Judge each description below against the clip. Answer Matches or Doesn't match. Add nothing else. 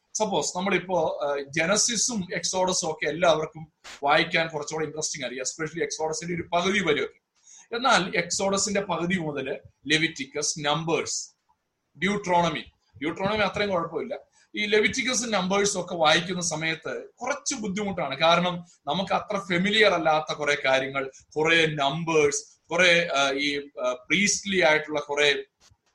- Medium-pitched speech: Matches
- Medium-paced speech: Matches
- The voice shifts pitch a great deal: Doesn't match